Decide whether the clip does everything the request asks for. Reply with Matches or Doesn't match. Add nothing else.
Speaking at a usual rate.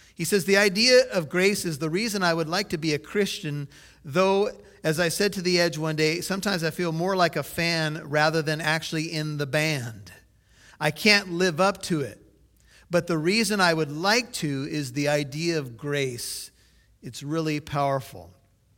Matches